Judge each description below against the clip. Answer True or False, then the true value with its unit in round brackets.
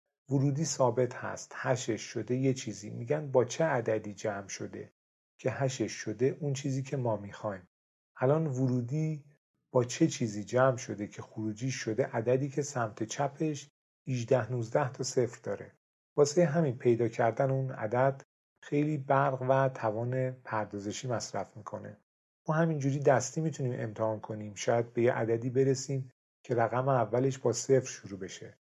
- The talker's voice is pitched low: True (125 Hz)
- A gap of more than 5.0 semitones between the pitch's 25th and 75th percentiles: False (3.7 semitones)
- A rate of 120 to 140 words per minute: False (150 wpm)